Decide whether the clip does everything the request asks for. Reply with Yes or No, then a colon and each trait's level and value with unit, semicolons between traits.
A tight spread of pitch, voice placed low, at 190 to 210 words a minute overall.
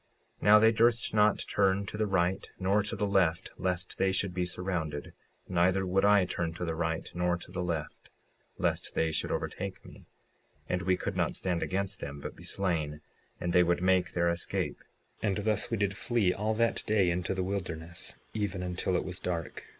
Yes: narrow, 2.3 semitones; very low, 90 Hz; average, 200 wpm